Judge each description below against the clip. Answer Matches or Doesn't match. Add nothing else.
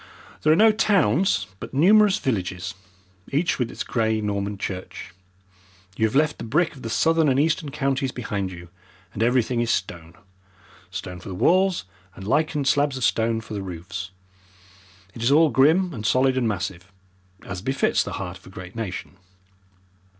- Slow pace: Doesn't match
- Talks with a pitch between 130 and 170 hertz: Doesn't match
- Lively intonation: Matches